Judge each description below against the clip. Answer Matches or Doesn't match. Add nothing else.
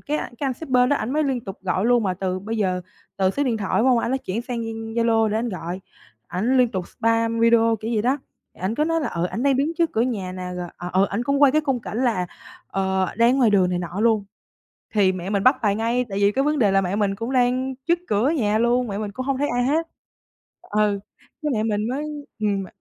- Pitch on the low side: Doesn't match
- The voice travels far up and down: Doesn't match